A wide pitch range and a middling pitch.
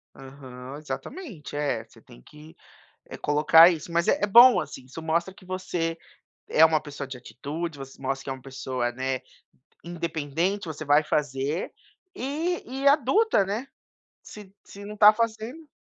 Yes: wide, 6.7 semitones; medium, 160 Hz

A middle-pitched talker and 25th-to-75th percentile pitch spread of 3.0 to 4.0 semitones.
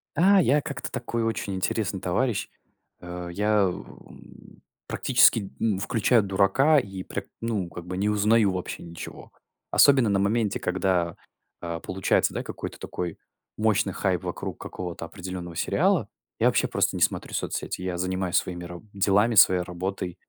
No: very low, 95 Hz; average, 3.4 semitones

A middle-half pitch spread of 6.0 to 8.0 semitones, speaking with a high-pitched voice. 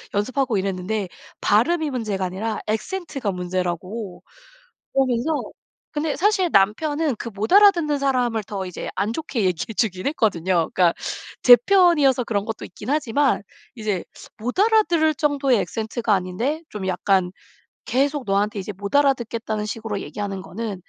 Yes: wide, 6.4 semitones; high, 225 Hz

